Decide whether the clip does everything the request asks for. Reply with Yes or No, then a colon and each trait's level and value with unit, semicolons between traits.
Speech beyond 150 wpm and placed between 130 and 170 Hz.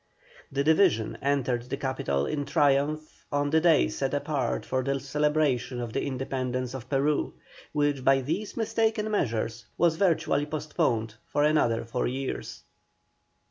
No: average, 140 wpm; medium, 140 Hz